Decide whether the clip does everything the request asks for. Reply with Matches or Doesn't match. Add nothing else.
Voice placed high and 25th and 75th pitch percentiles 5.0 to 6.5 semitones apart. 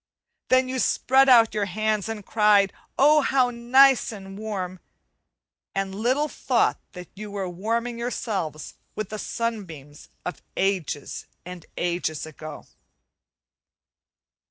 Doesn't match